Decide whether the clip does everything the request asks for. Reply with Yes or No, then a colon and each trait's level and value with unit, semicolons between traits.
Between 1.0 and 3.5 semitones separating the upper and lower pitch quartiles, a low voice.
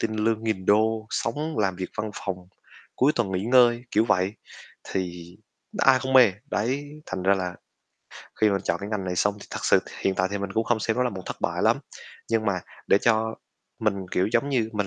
Yes: average, 3.2 semitones; low, 105 Hz